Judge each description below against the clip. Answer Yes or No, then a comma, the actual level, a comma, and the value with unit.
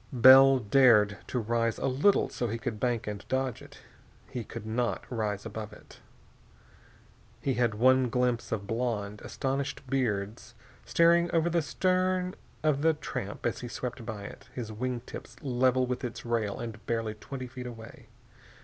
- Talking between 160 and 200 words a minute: Yes, average, 165 wpm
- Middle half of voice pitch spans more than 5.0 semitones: No, average, 3.0 semitones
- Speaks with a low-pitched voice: Yes, low, 120 Hz